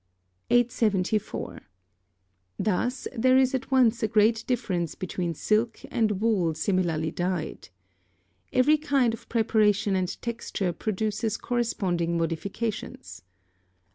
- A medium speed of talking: No, slow, 105 wpm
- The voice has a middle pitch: No, high, 215 Hz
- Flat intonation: No, average, 4.5 semitones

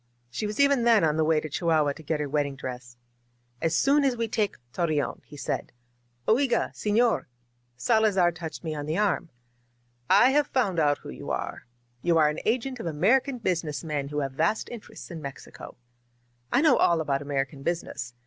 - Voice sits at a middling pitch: Yes, medium, 165 Hz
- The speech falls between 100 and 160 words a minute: No, average, 190 wpm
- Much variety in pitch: Yes, wide, 7.1 semitones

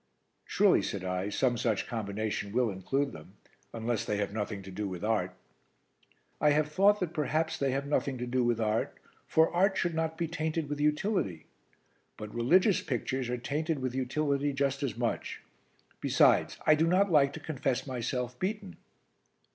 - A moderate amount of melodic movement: No, wide, 5.8 semitones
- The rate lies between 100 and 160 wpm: No, average, 170 wpm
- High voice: No, low, 135 Hz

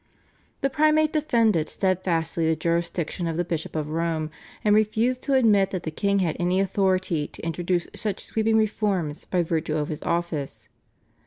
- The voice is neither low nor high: Yes, medium, 180 Hz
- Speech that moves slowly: No, average, 165 wpm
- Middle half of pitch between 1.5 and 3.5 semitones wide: No, average, 4.5 semitones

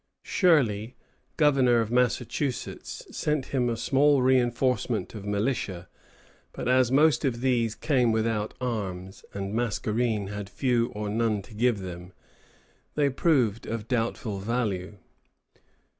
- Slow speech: Yes, slow, 130 wpm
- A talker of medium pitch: No, low, 115 Hz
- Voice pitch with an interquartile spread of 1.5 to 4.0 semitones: Yes, average, 3.6 semitones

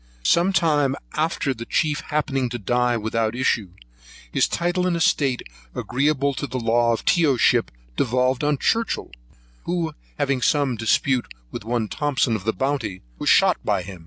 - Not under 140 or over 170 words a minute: Yes, average, 160 wpm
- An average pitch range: Yes, average, 4.1 semitones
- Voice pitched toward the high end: No, low, 130 Hz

